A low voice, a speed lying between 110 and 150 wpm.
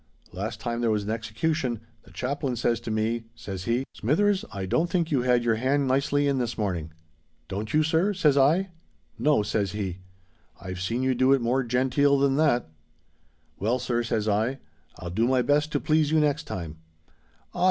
No: low, 120 Hz; average, 175 wpm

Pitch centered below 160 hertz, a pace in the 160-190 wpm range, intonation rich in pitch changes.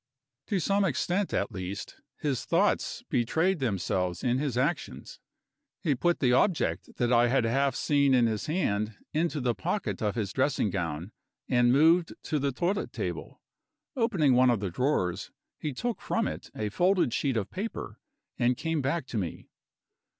Yes: low, 135 Hz; average, 165 wpm; wide, 6.7 semitones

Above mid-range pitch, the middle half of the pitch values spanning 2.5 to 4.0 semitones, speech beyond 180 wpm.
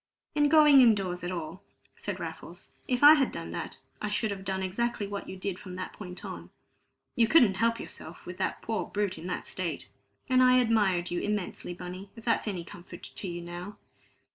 No: high, 200 Hz; average, 4.4 semitones; fast, 205 wpm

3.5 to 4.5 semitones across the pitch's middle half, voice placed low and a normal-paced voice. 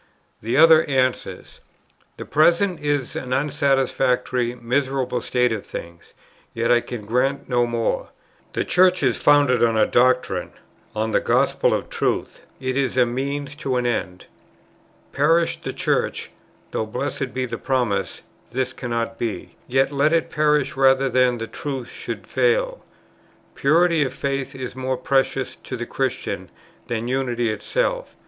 No: average, 2.8 semitones; low, 130 Hz; average, 150 wpm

